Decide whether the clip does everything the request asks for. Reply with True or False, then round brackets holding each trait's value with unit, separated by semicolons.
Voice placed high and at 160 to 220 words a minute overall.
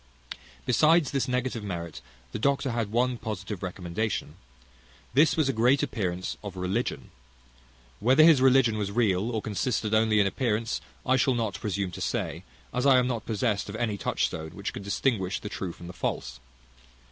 False (110 Hz; 170 wpm)